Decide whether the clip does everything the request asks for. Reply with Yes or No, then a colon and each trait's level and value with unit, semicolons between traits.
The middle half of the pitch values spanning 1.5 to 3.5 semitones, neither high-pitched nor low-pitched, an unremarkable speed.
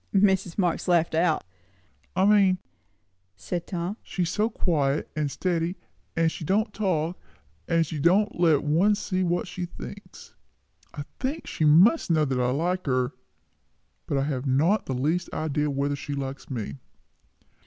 No: average, 4.3 semitones; medium, 165 Hz; average, 155 wpm